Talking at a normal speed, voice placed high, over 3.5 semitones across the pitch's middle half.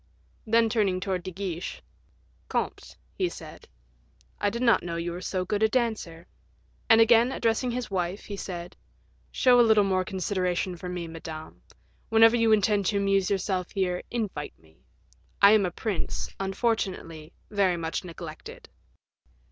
Yes: average, 155 wpm; high, 195 Hz; average, 3.9 semitones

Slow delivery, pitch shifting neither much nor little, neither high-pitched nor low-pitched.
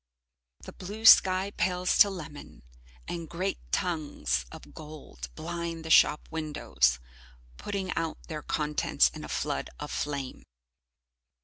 Yes: slow, 125 wpm; average, 3.6 semitones; medium, 160 Hz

